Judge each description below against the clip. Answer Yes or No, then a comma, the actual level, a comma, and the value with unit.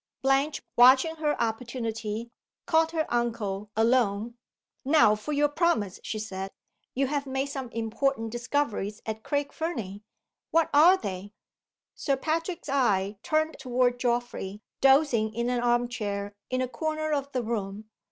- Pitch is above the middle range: Yes, high, 245 Hz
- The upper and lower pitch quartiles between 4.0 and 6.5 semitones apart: Yes, average, 4.7 semitones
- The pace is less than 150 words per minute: Yes, average, 140 wpm